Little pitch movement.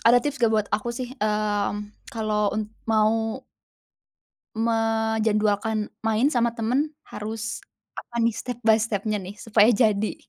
Yes: narrow, 1.5 semitones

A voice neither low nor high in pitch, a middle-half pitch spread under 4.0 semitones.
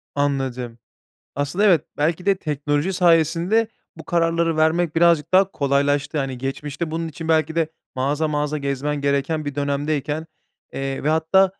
Yes: medium, 150 Hz; average, 2.7 semitones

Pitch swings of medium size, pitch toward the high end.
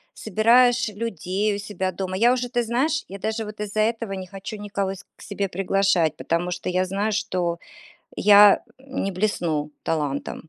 Yes: average, 3.0 semitones; high, 200 Hz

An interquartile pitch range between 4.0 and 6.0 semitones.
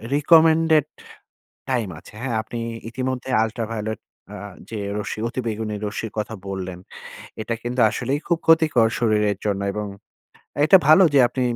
Yes: average, 4.6 semitones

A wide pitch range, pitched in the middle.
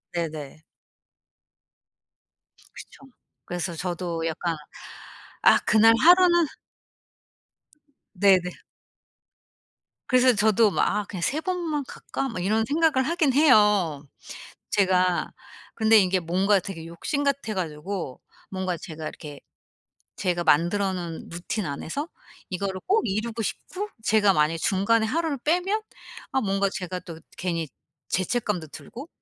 No: wide, 6.6 semitones; high, 195 Hz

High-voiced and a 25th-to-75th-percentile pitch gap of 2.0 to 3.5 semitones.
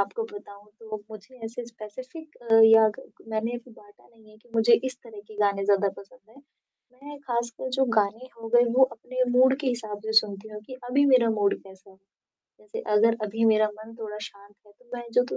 Yes: high, 225 Hz; average, 2.9 semitones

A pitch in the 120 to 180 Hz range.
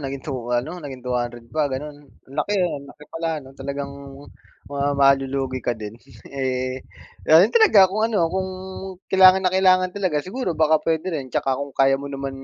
Yes: medium, 140 Hz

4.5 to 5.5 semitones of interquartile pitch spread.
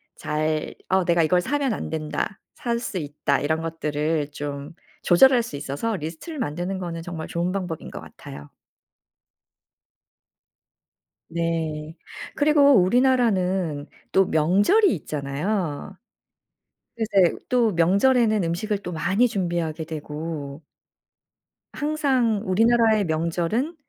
No: wide, 6.1 semitones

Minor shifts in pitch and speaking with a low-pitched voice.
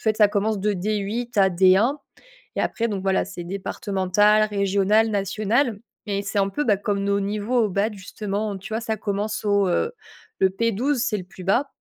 No: narrow, 1.9 semitones; high, 205 Hz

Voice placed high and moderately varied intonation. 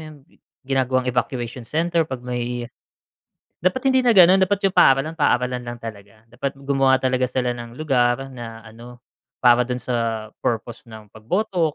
No: low, 125 Hz; average, 4.0 semitones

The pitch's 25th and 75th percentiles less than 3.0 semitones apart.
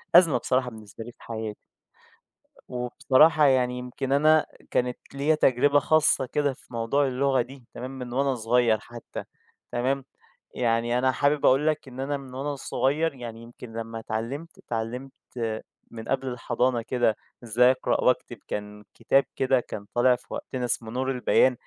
Yes: narrow, 2.6 semitones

